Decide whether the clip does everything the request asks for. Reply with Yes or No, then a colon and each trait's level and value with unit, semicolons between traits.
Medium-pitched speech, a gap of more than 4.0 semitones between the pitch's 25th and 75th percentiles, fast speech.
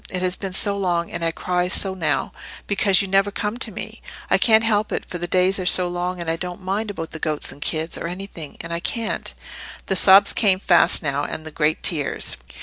No: medium, 180 Hz; average, 2.8 semitones; fast, 230 wpm